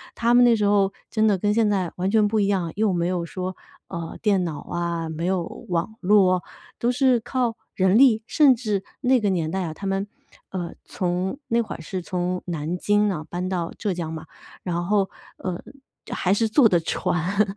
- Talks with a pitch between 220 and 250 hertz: No, high, 190 Hz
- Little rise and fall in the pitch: No, average, 3.5 semitones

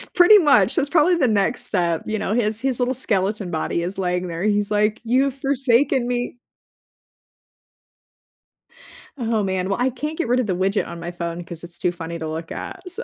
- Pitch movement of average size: No, wide, 6.3 semitones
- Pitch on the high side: Yes, high, 210 Hz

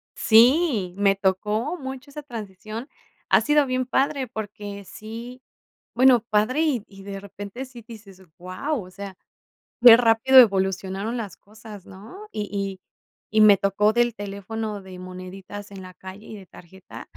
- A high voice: Yes, high, 210 Hz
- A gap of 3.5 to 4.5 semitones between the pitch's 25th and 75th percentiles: Yes, average, 3.8 semitones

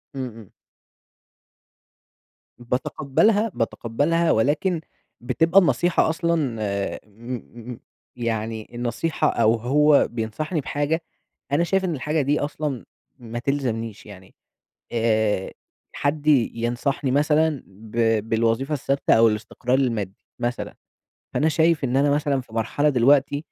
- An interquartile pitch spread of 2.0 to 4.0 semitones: No, average, 4.8 semitones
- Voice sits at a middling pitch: No, low, 130 Hz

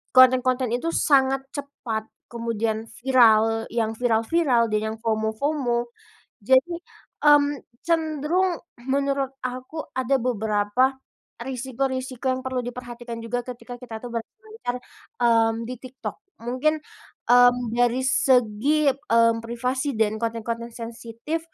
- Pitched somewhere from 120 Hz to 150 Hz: No, high, 245 Hz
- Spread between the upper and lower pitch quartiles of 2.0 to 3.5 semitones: Yes, average, 2.8 semitones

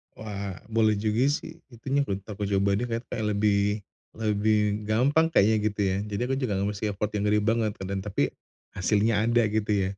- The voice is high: No, low, 105 Hz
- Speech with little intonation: Yes, narrow, 2.2 semitones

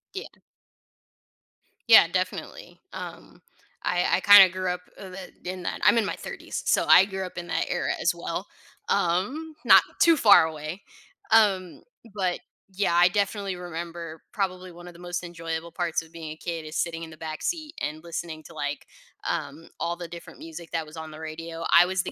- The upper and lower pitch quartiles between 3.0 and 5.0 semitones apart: No, narrow, 2.4 semitones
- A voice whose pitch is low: No, medium, 175 Hz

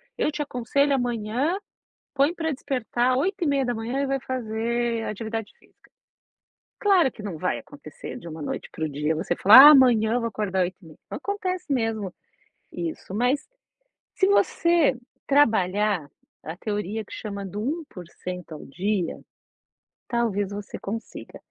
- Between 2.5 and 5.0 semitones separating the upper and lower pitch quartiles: No, wide, 5.6 semitones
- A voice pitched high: Yes, high, 230 Hz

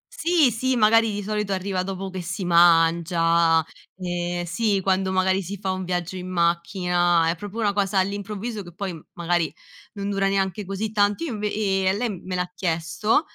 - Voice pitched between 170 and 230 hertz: Yes, high, 190 Hz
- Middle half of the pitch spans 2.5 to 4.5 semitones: Yes, average, 2.8 semitones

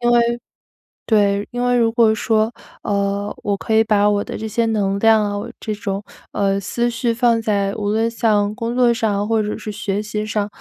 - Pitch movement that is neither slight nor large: No, narrow, 2.1 semitones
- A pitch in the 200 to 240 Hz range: Yes, high, 215 Hz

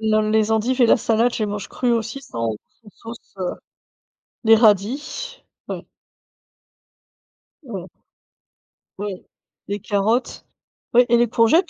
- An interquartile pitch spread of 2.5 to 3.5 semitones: Yes, average, 2.8 semitones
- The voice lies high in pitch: Yes, high, 225 Hz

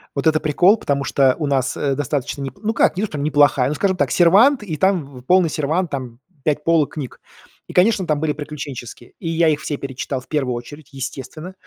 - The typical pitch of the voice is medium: Yes, medium, 150 Hz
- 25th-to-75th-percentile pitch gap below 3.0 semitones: No, average, 3.6 semitones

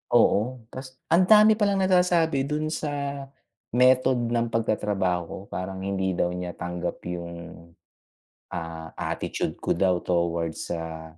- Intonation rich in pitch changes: Yes, wide, 8.1 semitones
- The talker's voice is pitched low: Yes, low, 100 Hz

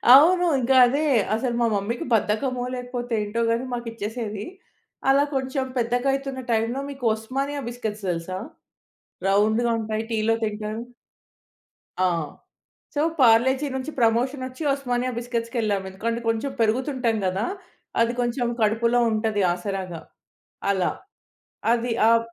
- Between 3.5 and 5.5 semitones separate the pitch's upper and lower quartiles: No, average, 2.9 semitones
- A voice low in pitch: No, high, 235 Hz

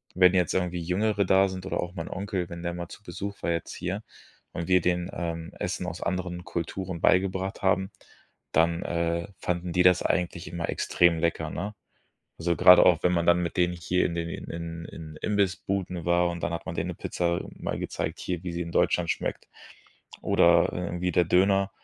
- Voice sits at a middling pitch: No, very low, 90 Hz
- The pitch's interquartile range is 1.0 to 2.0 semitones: Yes, narrow, 1.5 semitones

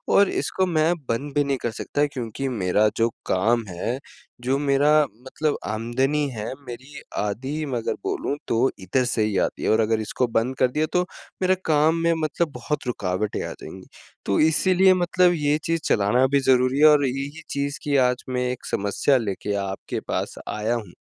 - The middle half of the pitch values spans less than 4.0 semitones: No, average, 4.8 semitones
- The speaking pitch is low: Yes, low, 130 Hz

